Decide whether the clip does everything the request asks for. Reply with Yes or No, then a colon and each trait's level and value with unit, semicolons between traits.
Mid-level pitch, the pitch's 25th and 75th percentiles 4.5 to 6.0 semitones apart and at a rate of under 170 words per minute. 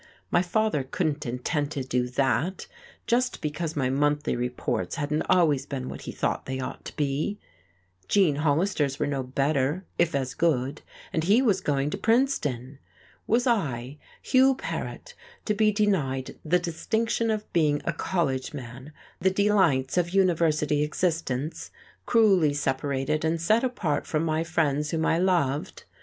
Yes: medium, 155 Hz; average, 5.3 semitones; average, 150 wpm